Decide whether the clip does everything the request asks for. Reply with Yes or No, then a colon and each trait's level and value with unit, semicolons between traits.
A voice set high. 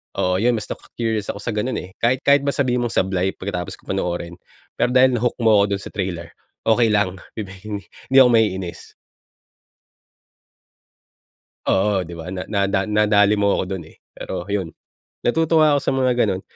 No: low, 105 Hz